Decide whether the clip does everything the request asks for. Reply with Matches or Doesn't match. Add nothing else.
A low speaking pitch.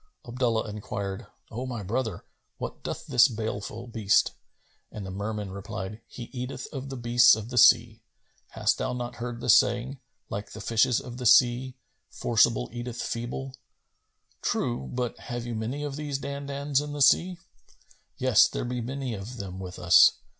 Matches